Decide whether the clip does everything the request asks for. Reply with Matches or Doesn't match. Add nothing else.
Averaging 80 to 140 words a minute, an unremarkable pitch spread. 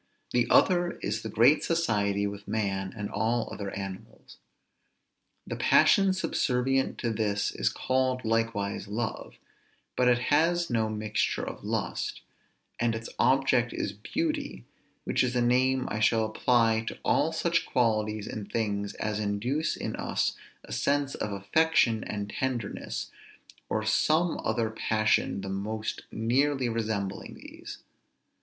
Matches